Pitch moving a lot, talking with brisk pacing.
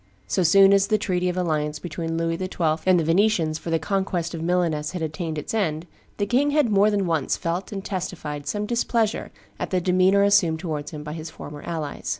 No: average, 3.8 semitones; fast, 210 wpm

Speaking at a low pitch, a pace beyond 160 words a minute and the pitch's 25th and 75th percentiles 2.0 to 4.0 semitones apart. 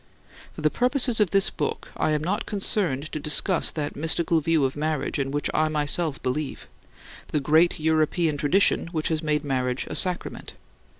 No: medium, 155 Hz; average, 175 wpm; average, 2.8 semitones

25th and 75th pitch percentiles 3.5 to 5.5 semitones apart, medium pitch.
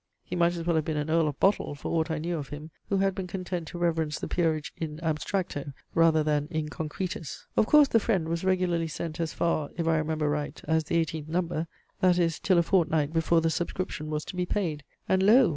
No: narrow, 2.5 semitones; medium, 165 Hz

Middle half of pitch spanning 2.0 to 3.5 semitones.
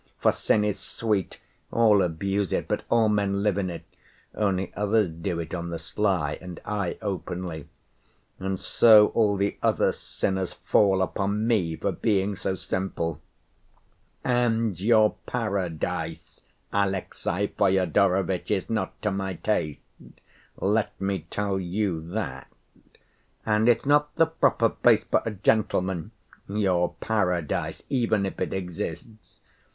Yes: average, 2.8 semitones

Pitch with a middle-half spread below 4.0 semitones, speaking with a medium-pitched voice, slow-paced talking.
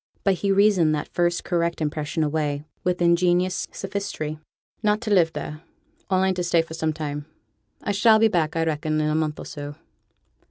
No: average, 3.5 semitones; medium, 170 Hz; average, 185 wpm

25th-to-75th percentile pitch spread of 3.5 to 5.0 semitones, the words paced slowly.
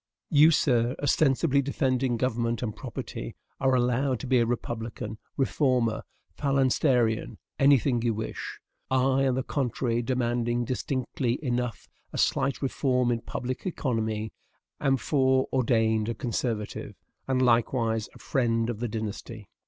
No: narrow, 2.4 semitones; slow, 130 wpm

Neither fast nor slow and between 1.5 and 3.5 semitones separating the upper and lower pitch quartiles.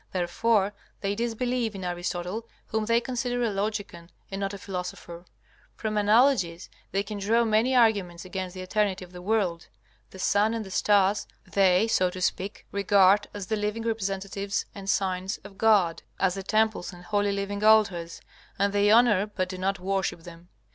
Yes: average, 175 wpm; average, 2.7 semitones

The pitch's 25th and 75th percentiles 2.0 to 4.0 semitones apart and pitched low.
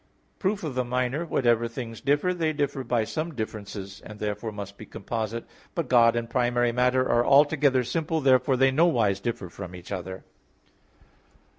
No: average, 4.4 semitones; low, 120 Hz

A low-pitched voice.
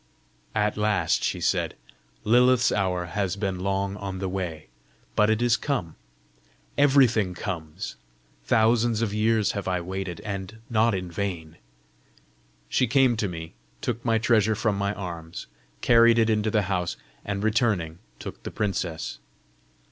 Yes: low, 105 Hz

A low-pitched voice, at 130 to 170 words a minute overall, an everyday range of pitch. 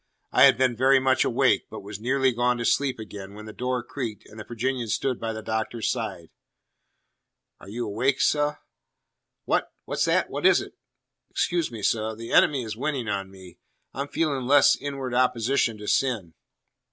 No: low, 120 Hz; average, 180 wpm; average, 3.5 semitones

